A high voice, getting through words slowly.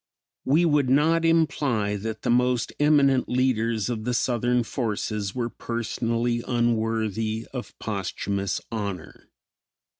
No: low, 120 Hz; slow, 115 wpm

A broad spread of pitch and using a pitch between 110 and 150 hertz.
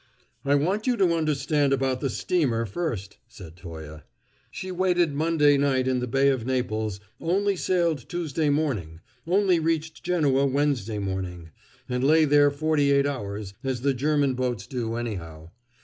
Yes: wide, 5.7 semitones; medium, 140 Hz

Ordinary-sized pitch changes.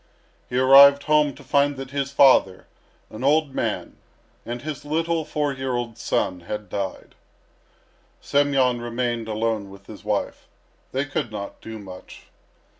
Yes: average, 4.2 semitones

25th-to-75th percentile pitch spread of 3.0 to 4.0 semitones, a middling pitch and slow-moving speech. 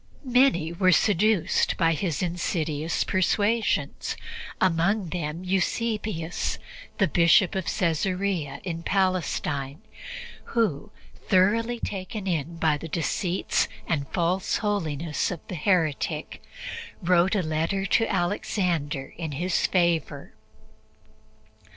Yes: average, 3.3 semitones; medium, 175 Hz; slow, 100 wpm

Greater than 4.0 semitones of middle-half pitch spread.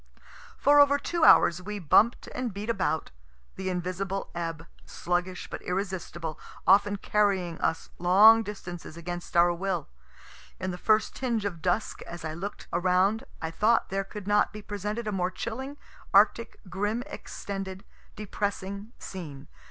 No: average, 3.1 semitones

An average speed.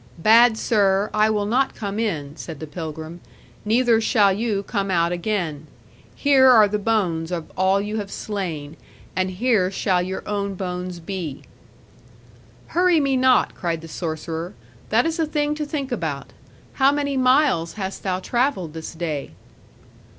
Yes: average, 160 wpm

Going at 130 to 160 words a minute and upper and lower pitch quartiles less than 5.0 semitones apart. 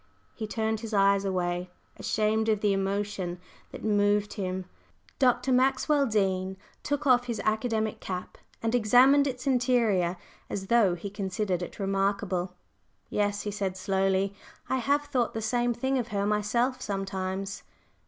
Yes: average, 145 wpm; average, 3.7 semitones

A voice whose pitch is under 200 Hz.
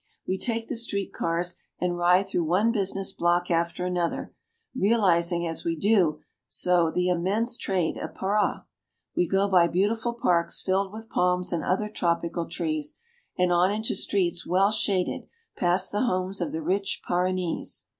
Yes: medium, 185 Hz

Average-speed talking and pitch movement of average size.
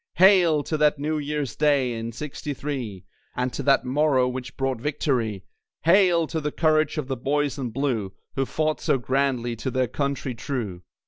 Yes: average, 180 wpm; average, 3.2 semitones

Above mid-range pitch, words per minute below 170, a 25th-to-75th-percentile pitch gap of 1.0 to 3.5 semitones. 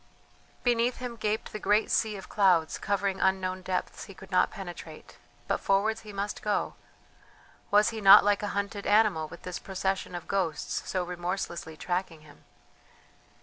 Yes: high, 195 Hz; average, 160 wpm; narrow, 2.6 semitones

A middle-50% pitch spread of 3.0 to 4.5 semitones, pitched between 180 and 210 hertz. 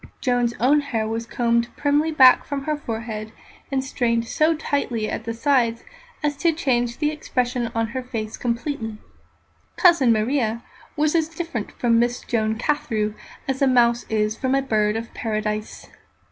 No: average, 4.0 semitones; high, 240 Hz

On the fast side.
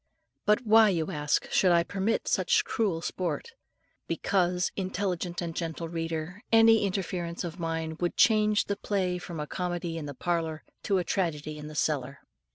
No: average, 165 wpm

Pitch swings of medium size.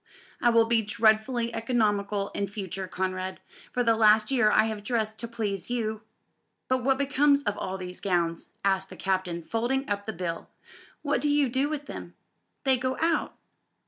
Yes: average, 4.3 semitones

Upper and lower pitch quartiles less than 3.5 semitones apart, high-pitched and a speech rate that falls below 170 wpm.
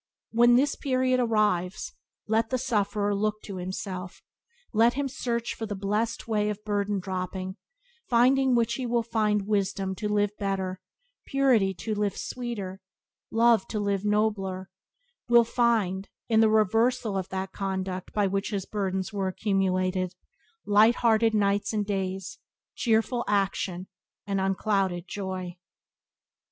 Yes: average, 3.0 semitones; high, 205 Hz; average, 140 wpm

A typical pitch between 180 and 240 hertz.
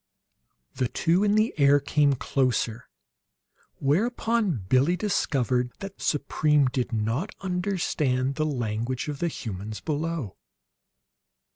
No: medium, 145 Hz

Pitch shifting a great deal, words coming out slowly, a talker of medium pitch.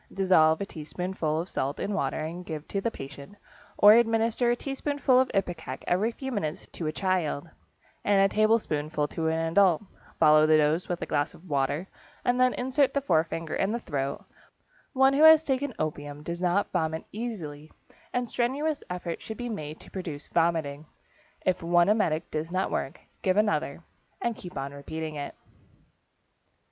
No: wide, 6.3 semitones; average, 175 wpm; medium, 175 Hz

